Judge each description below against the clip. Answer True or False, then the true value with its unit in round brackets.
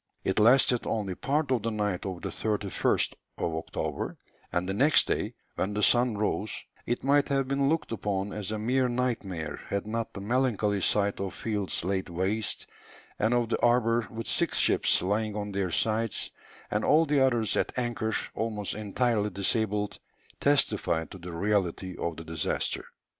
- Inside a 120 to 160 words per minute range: False (170 wpm)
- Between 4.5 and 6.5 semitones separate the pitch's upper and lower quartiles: False (3.6 semitones)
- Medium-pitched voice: False (105 Hz)